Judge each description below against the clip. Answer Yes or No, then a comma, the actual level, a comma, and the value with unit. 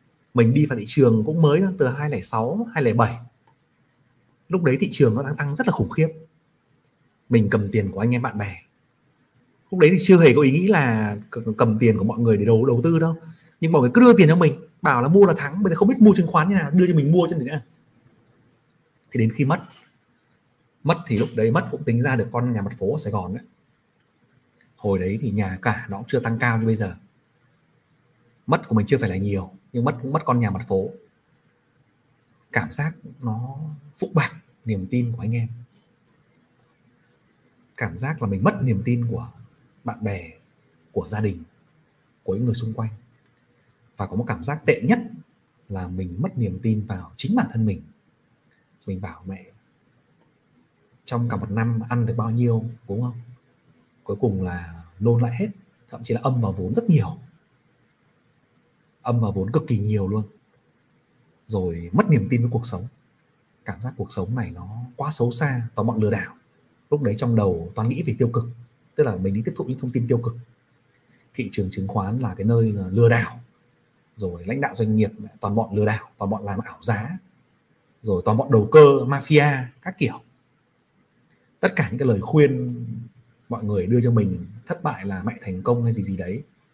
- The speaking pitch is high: No, low, 120 Hz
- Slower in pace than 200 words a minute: No, average, 205 wpm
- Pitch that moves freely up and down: No, average, 5.0 semitones